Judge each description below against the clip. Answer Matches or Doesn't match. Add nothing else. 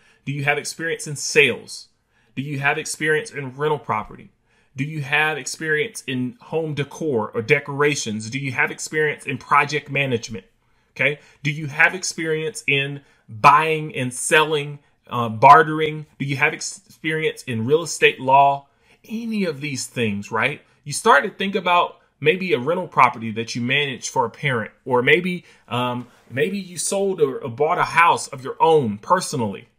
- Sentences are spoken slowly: Doesn't match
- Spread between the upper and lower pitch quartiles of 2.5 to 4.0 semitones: Matches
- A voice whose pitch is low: Doesn't match